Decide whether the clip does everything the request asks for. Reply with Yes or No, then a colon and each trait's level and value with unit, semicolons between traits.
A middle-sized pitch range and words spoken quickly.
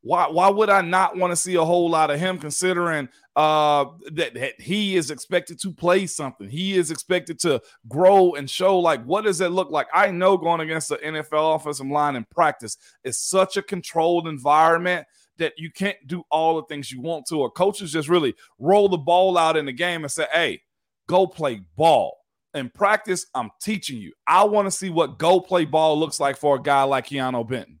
Yes: average, 3.7 semitones; fast, 215 wpm